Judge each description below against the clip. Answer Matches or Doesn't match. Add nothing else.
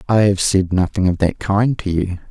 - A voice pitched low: Matches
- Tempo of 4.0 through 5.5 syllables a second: Matches